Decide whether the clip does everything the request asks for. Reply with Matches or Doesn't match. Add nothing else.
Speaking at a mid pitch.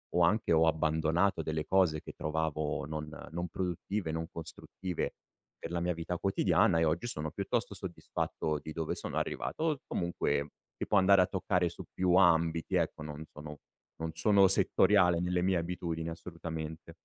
Doesn't match